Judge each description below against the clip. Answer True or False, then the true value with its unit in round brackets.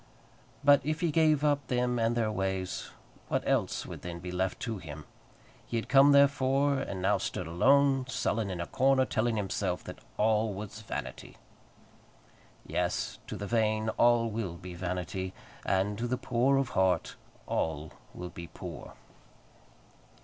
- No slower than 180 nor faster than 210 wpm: False (155 wpm)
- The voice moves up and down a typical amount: False (5.9 semitones)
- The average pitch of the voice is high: False (110 Hz)